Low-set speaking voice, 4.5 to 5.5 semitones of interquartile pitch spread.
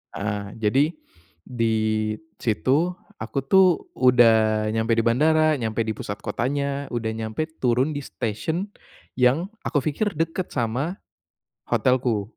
Yes: low, 120 Hz; average, 5.0 semitones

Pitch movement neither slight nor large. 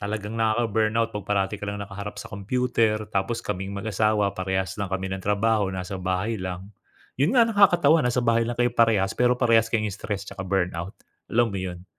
Yes: average, 3.1 semitones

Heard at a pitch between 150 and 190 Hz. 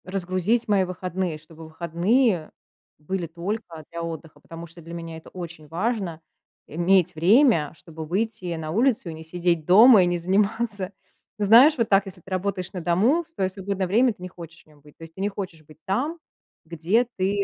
Yes: medium, 185 Hz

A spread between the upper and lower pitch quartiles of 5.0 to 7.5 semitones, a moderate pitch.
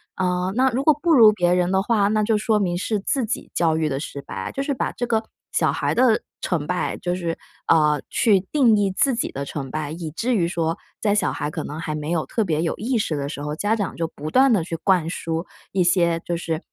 Yes: average, 5.3 semitones; medium, 180 Hz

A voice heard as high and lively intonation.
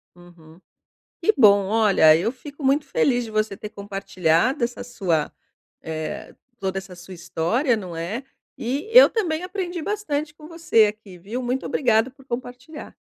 Yes: high, 225 Hz; wide, 6.8 semitones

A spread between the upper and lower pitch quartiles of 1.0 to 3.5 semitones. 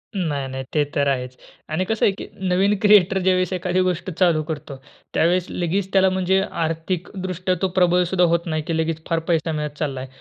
Yes: average, 2.9 semitones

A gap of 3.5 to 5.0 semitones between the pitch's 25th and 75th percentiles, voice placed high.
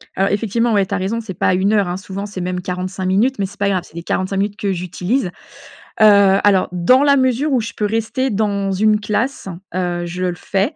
No: average, 2.9 semitones; high, 200 Hz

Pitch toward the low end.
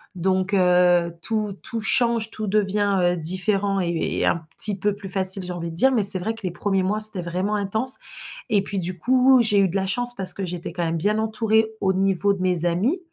No: high, 195 Hz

